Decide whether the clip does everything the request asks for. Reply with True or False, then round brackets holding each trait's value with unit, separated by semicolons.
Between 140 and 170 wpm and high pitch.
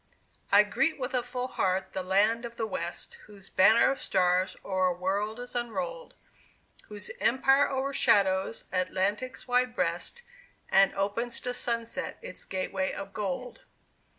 True (145 wpm; 220 Hz)